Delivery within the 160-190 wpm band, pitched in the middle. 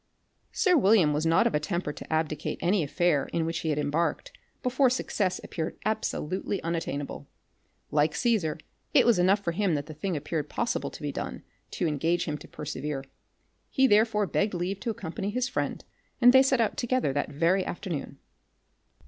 Yes: average, 180 wpm; medium, 175 Hz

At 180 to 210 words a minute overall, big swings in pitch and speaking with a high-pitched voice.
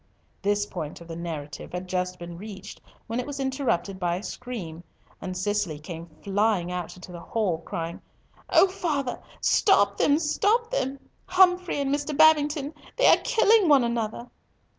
No: average, 155 wpm; wide, 8.3 semitones; high, 210 Hz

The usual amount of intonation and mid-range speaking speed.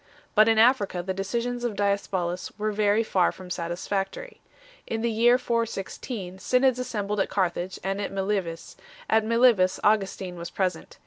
Yes: average, 3.6 semitones; average, 155 wpm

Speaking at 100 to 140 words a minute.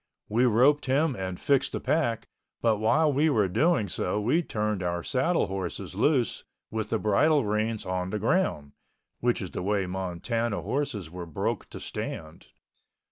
No: average, 165 wpm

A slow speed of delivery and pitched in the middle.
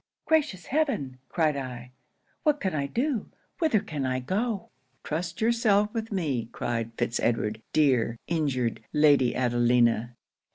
Yes: slow, 130 wpm; medium, 150 Hz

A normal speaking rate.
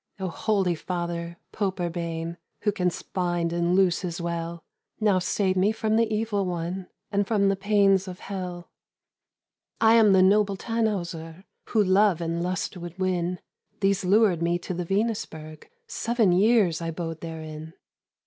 Yes: average, 155 wpm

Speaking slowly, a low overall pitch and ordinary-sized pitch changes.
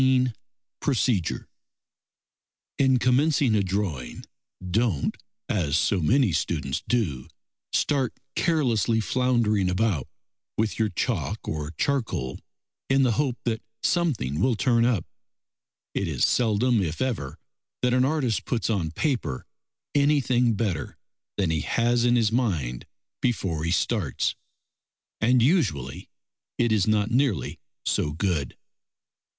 No: slow, 120 wpm; low, 115 Hz; wide, 6.4 semitones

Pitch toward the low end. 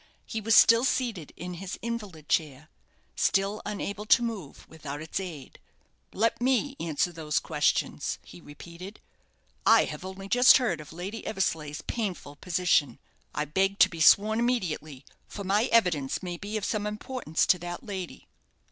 No: high, 190 Hz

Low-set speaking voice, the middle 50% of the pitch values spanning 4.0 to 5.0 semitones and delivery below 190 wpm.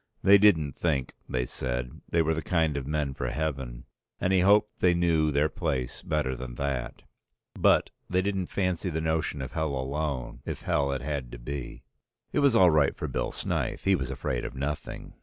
No: very low, 75 Hz; average, 4.4 semitones; average, 195 wpm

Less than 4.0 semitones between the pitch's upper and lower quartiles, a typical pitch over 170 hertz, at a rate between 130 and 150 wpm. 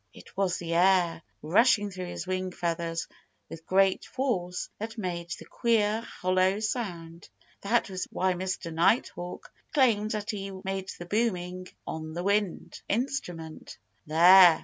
Yes: average, 3.1 semitones; medium, 185 Hz; average, 140 wpm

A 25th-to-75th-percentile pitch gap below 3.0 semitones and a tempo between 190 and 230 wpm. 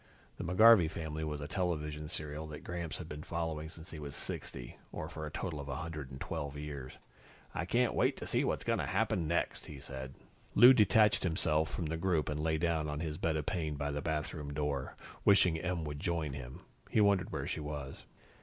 Yes: narrow, 2.4 semitones; fast, 205 wpm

